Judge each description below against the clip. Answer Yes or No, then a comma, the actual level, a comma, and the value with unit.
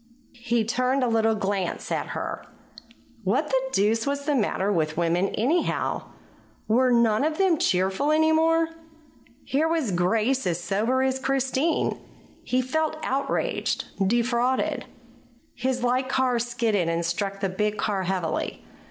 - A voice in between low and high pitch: No, high, 240 Hz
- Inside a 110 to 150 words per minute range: Yes, average, 140 wpm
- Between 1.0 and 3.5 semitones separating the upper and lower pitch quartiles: No, average, 5.2 semitones